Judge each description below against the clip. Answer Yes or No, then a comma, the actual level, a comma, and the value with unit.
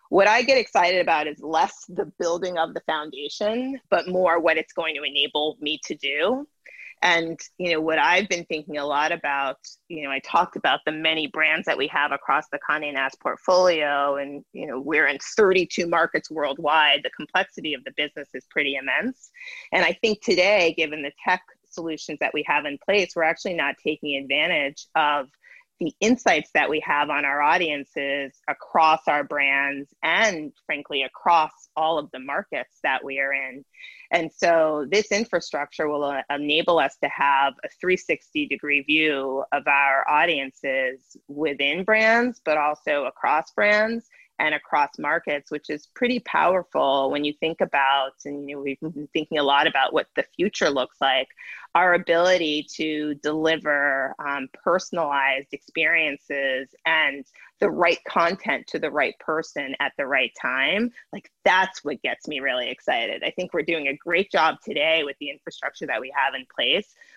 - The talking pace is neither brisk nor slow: Yes, average, 175 wpm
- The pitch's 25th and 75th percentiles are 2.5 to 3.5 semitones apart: No, average, 4.1 semitones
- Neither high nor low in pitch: Yes, medium, 155 Hz